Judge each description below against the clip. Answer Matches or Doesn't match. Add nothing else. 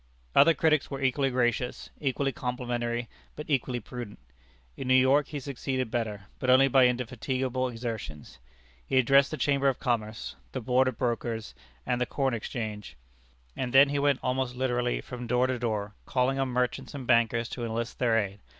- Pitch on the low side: Matches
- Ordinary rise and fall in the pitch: Doesn't match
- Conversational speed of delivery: Matches